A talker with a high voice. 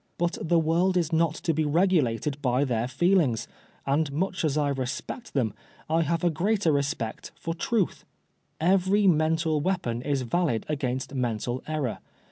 No: medium, 155 Hz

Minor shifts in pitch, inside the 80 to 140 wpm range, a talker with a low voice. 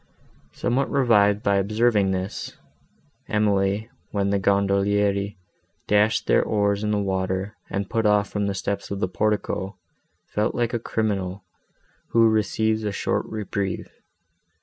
Yes: narrow, 1.5 semitones; slow, 135 wpm; low, 100 Hz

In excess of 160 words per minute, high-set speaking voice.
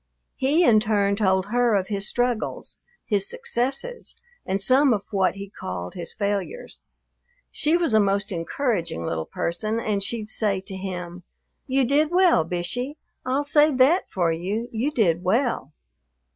No: average, 155 wpm; high, 215 Hz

